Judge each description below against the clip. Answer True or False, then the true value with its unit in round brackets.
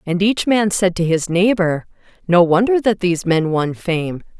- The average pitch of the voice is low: False (185 Hz)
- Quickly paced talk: False (190 wpm)